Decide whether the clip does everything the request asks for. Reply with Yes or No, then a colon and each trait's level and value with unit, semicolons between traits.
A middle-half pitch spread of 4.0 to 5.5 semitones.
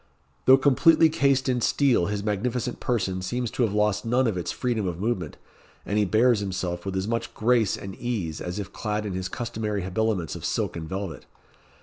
Yes: average, 4.4 semitones